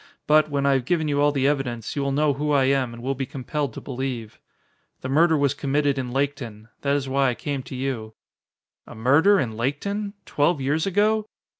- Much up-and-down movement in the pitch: No, narrow, 2.4 semitones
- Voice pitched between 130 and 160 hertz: Yes, medium, 140 Hz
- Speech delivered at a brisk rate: Yes, fast, 210 wpm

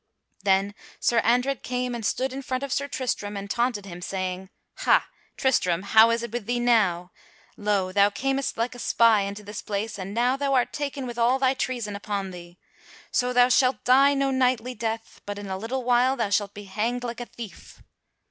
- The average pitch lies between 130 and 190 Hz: No, high, 235 Hz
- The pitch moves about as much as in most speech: Yes, average, 3.9 semitones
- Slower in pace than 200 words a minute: No, fast, 205 wpm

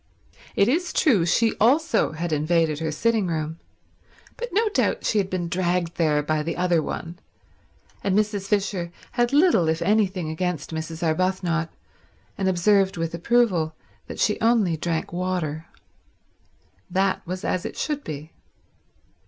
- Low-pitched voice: No, medium, 180 Hz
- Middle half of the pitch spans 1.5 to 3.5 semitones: No, average, 4.2 semitones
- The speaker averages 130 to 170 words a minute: Yes, average, 145 wpm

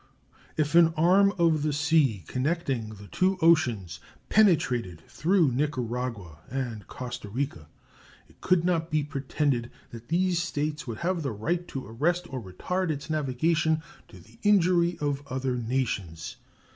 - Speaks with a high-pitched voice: No, medium, 145 Hz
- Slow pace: No, average, 145 wpm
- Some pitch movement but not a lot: No, wide, 5.9 semitones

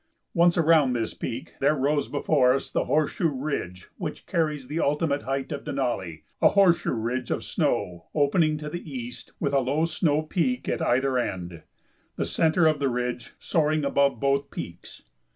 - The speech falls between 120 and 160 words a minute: No, average, 170 wpm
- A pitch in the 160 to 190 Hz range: No, medium, 140 Hz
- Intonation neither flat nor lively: Yes, average, 3.8 semitones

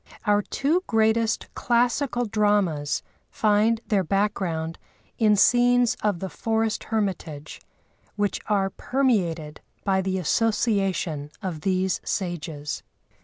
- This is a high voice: Yes, high, 205 Hz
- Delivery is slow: Yes, slow, 105 wpm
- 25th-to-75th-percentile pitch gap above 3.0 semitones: Yes, average, 4.0 semitones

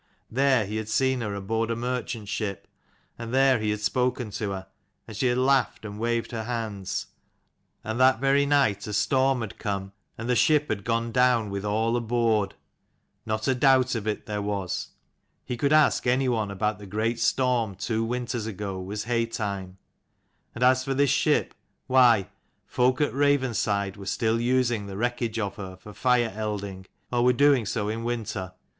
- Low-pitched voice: Yes, low, 115 Hz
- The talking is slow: No, average, 180 wpm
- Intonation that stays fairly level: No, average, 3.3 semitones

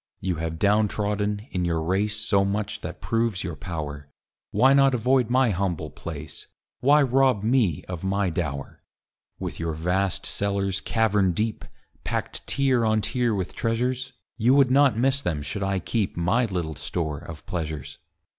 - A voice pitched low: Yes, low, 100 Hz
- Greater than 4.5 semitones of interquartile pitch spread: Yes, wide, 5.4 semitones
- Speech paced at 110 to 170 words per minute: Yes, average, 165 wpm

